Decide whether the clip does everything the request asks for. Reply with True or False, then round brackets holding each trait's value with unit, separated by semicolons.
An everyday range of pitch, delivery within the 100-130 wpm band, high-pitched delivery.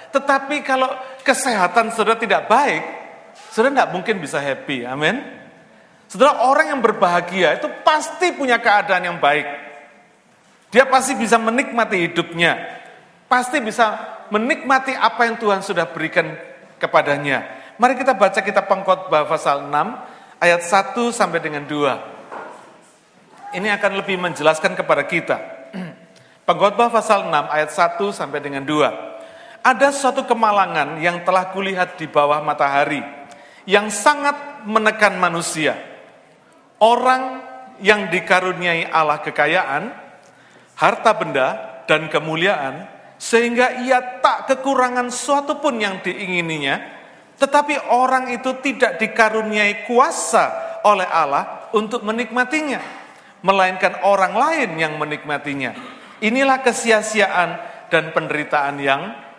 False (7.0 semitones; 115 wpm; 205 Hz)